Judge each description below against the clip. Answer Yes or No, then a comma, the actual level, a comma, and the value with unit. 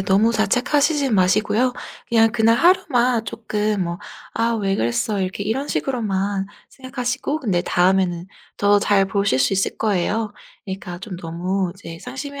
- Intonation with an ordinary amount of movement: Yes, average, 3.9 semitones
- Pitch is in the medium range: No, high, 205 Hz